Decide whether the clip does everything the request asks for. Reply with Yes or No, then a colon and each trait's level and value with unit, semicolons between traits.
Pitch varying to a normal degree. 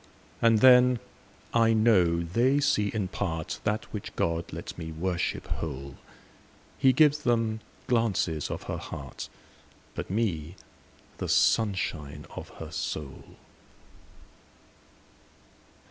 No: wide, 5.9 semitones